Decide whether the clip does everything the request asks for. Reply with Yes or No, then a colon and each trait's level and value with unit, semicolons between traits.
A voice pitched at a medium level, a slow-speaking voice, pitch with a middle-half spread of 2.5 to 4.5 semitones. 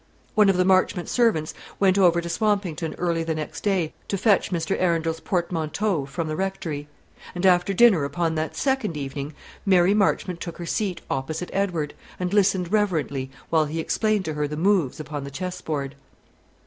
No: medium, 175 Hz; average, 175 wpm; average, 3.7 semitones